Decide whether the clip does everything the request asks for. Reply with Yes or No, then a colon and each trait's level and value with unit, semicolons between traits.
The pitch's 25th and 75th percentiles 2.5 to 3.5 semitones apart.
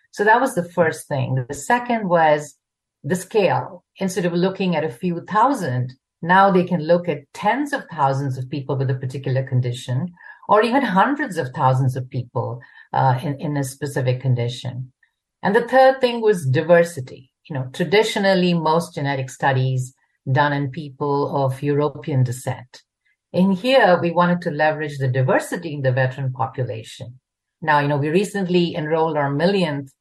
No: average, 5.3 semitones